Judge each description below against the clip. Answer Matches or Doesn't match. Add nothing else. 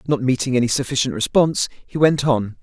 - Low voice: Matches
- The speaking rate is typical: Matches